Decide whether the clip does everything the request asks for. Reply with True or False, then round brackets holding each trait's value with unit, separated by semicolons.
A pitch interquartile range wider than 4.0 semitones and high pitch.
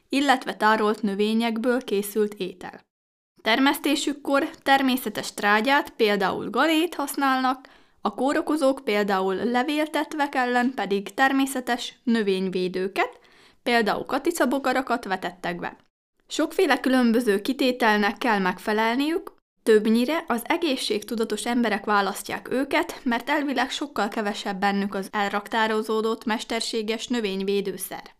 True (4.7 semitones; 235 Hz)